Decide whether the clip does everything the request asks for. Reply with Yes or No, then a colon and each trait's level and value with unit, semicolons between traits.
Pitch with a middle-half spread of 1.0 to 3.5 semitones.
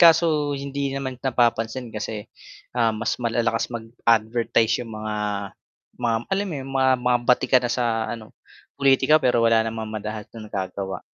Yes: average, 3.0 semitones